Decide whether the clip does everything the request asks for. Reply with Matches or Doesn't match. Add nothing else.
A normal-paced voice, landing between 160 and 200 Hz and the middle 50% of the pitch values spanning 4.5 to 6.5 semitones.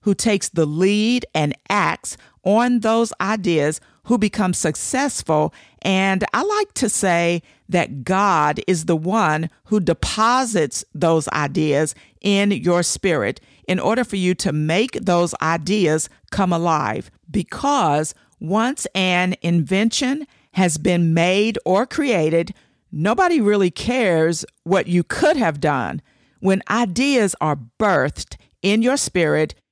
Doesn't match